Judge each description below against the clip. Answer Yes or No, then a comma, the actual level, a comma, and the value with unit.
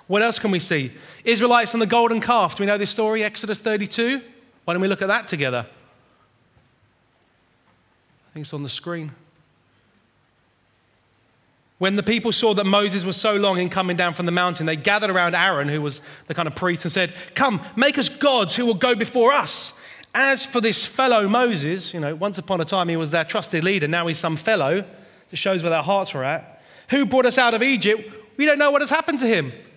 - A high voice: Yes, high, 195 Hz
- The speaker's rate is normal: No, fast, 215 wpm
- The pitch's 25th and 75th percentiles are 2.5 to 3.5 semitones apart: No, wide, 5.5 semitones